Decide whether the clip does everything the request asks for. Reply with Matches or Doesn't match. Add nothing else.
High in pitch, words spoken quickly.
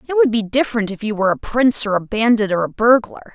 Matches